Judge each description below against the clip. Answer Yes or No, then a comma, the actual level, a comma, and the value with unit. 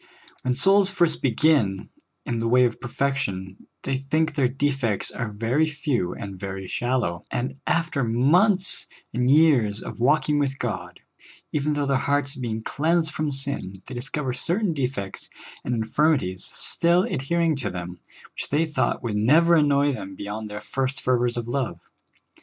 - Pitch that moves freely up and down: No, average, 5.0 semitones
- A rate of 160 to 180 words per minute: Yes, average, 165 wpm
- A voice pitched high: No, low, 130 Hz